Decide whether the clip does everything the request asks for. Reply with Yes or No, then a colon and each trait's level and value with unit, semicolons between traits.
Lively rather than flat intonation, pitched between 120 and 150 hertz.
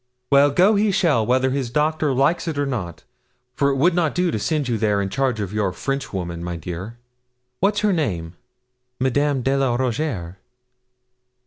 Yes: wide, 6.2 semitones; low, 135 Hz